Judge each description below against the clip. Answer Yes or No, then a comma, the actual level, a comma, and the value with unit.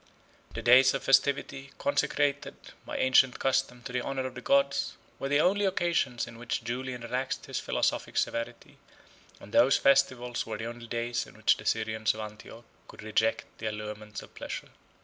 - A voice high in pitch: No, low, 125 Hz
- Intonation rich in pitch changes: No, average, 3.0 semitones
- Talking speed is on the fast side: No, average, 175 wpm